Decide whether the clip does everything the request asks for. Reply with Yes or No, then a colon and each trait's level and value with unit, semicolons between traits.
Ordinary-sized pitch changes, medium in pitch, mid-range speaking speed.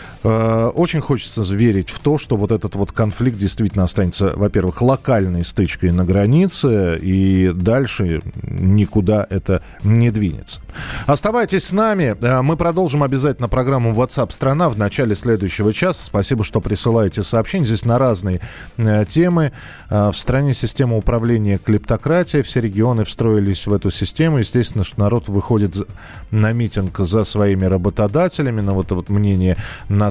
No: average, 4.6 semitones; low, 110 Hz; average, 140 wpm